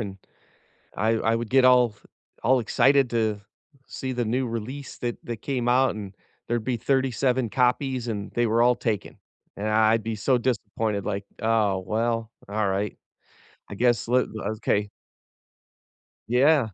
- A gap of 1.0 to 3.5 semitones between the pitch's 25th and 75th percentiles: Yes, average, 2.8 semitones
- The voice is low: Yes, low, 115 Hz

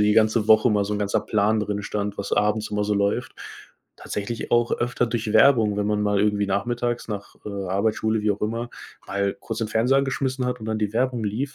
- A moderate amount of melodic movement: No, narrow, 2.3 semitones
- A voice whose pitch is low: Yes, low, 110 Hz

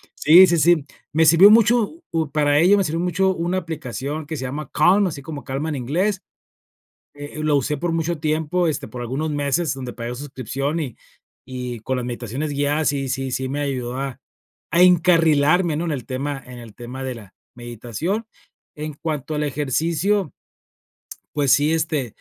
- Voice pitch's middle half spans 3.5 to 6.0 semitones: Yes, average, 3.9 semitones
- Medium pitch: Yes, medium, 150 Hz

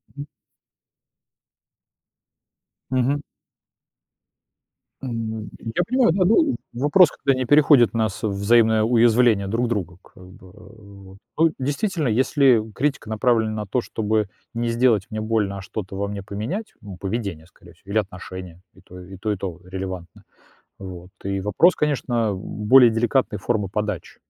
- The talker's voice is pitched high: No, low, 110 Hz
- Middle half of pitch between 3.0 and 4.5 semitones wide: Yes, average, 4.1 semitones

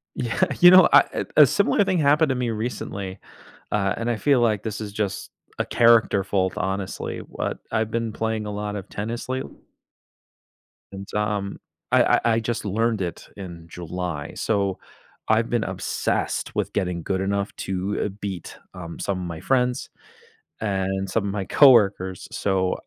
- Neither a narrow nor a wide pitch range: Yes, average, 3.3 semitones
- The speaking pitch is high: No, low, 105 Hz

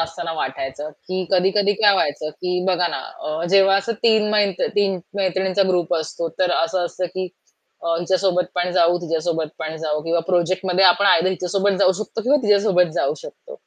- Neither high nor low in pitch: Yes, medium, 180 Hz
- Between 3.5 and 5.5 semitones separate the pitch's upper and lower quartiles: No, narrow, 2.6 semitones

